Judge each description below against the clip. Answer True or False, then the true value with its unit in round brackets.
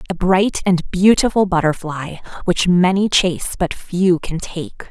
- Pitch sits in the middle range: True (180 Hz)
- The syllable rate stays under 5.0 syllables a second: True (4.2 syllables/s)